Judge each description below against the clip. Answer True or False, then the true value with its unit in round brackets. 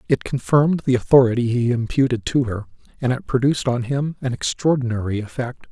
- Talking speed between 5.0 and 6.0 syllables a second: True (5.8 syllables/s)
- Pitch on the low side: True (125 Hz)